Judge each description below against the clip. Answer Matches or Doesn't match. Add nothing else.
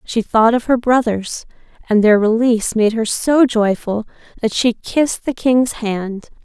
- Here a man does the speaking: Doesn't match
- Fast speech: Doesn't match